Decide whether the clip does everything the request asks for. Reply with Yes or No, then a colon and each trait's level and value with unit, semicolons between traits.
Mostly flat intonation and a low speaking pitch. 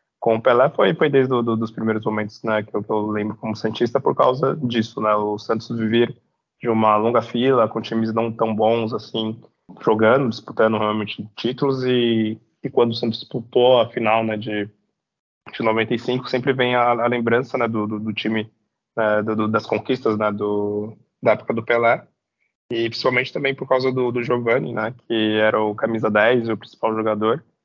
Yes: narrow, 1.7 semitones; low, 115 Hz